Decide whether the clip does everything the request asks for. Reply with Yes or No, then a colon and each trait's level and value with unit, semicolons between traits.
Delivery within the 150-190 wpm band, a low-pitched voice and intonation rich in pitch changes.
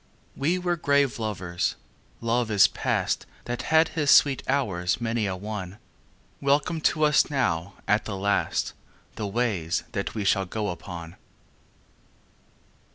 No: slow, 135 wpm; low, 110 Hz; wide, 6.5 semitones